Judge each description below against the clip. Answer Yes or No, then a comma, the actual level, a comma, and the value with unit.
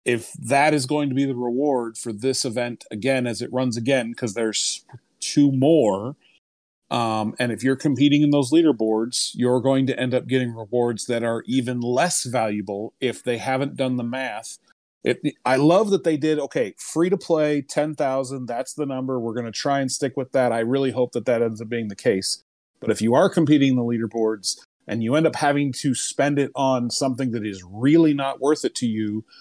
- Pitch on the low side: Yes, low, 130 Hz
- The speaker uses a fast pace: Yes, fast, 215 wpm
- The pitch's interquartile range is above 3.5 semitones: No, average, 3.2 semitones